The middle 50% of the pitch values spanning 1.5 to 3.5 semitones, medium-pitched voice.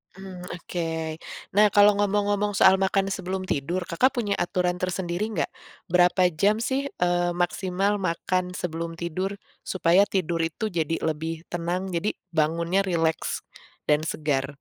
Yes: narrow, 2.6 semitones; medium, 180 Hz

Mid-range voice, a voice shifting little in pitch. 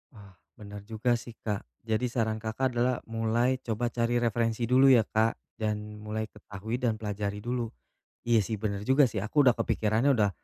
No: low, 110 Hz; narrow, 2.2 semitones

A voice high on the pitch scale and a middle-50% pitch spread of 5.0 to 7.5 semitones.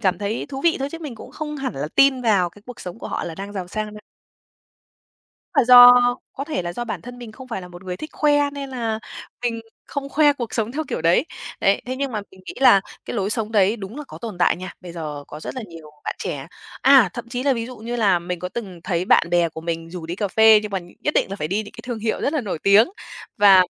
Yes: high, 215 Hz; wide, 5.6 semitones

